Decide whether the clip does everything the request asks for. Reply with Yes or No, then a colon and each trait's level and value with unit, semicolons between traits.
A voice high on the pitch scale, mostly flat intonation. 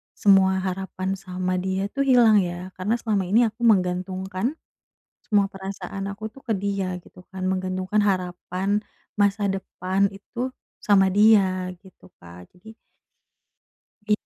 Yes: high, 195 Hz; narrow, 2.0 semitones